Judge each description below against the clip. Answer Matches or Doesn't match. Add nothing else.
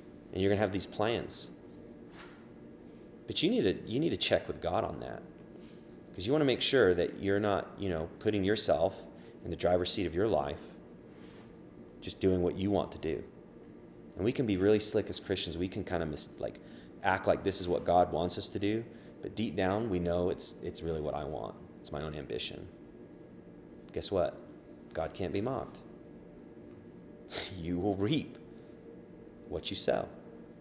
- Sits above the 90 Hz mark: Doesn't match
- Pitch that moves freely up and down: Matches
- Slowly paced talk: Doesn't match